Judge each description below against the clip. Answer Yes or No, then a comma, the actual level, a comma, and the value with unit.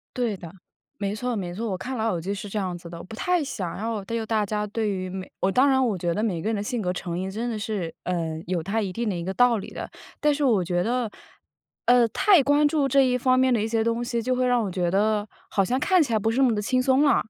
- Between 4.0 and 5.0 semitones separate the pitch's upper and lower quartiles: Yes, average, 4.6 semitones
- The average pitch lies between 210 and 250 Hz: Yes, high, 220 Hz